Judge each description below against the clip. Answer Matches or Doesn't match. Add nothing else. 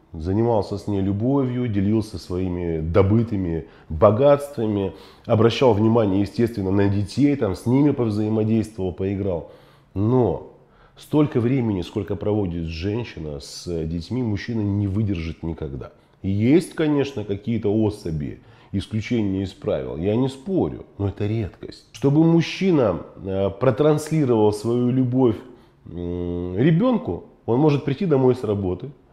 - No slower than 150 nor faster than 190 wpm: Doesn't match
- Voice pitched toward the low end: Matches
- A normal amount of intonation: Matches